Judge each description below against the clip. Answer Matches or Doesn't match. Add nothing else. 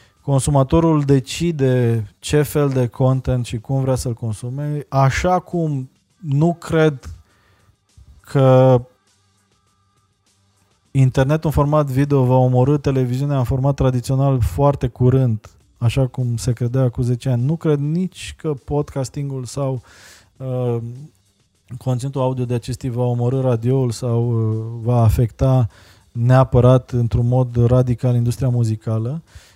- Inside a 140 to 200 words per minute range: Doesn't match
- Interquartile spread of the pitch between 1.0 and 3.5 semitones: Matches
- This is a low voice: Matches